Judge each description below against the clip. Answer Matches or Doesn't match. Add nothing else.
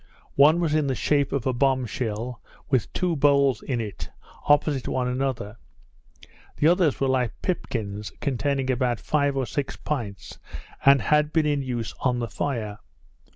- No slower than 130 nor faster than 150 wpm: Doesn't match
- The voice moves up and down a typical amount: Matches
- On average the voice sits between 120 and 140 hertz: Matches